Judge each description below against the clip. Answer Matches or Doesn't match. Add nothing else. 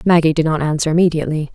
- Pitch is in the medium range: Matches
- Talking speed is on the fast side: Doesn't match